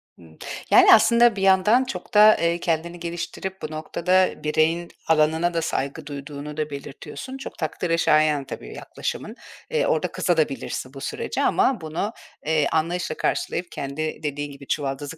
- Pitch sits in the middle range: Yes, medium, 160 Hz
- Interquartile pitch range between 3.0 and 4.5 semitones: Yes, average, 3.3 semitones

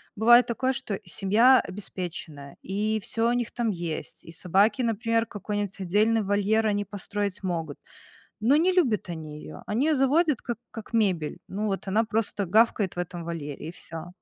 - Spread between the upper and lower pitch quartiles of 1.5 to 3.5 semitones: No, average, 4.1 semitones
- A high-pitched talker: Yes, high, 205 Hz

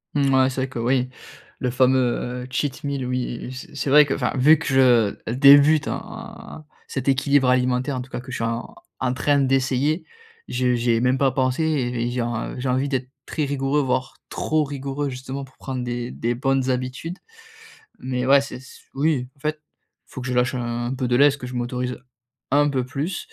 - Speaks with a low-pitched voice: Yes, low, 130 Hz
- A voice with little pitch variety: Yes, narrow, 2.0 semitones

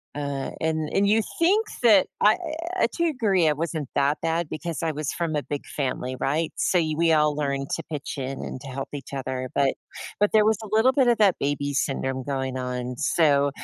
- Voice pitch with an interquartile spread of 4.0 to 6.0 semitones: Yes, average, 4.7 semitones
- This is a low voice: No, medium, 150 Hz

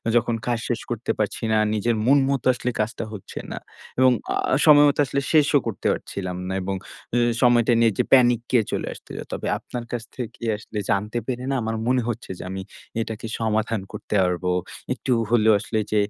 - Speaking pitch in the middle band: No, low, 115 Hz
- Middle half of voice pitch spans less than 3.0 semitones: Yes, narrow, 2.5 semitones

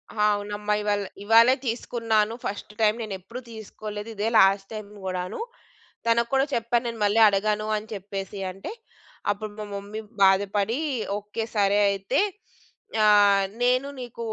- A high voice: Yes, high, 210 Hz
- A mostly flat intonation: Yes, narrow, 2.1 semitones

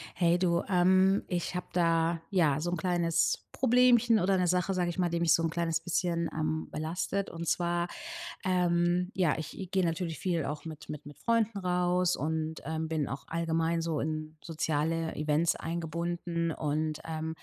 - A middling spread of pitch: No, narrow, 2.0 semitones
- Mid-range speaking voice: Yes, medium, 170 Hz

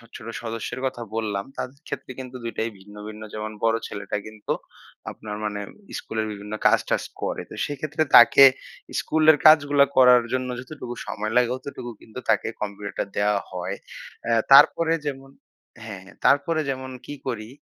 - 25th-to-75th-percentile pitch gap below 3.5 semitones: No, average, 4.3 semitones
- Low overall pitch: Yes, low, 120 Hz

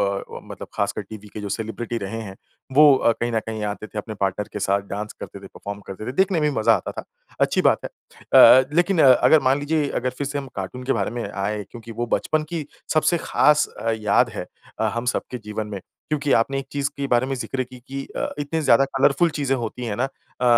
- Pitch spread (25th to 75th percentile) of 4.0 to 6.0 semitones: Yes, average, 4.7 semitones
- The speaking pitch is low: Yes, low, 125 Hz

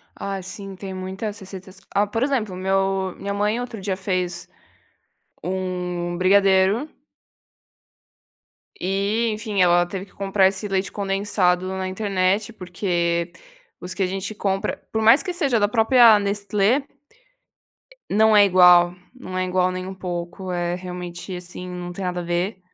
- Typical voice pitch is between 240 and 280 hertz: No, high, 190 Hz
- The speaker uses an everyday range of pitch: No, narrow, 2.2 semitones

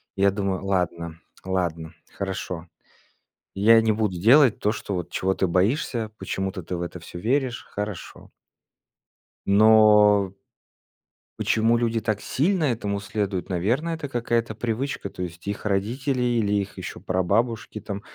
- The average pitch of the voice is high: No, low, 105 Hz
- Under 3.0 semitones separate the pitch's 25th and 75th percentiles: No, average, 3.5 semitones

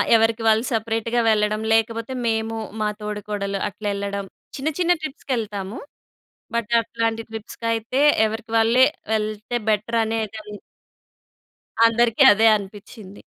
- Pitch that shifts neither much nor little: No, narrow, 1.5 semitones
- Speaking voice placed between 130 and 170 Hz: No, high, 220 Hz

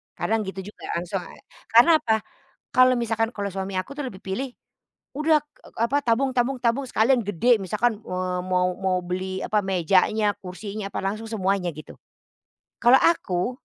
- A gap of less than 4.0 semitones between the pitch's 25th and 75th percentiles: No, average, 4.4 semitones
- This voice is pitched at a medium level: No, high, 215 Hz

